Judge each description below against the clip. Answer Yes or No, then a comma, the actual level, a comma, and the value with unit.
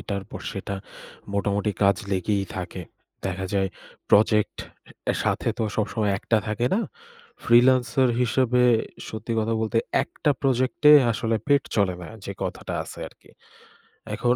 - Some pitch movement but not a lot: Yes, average, 3.7 semitones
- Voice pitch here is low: Yes, low, 110 Hz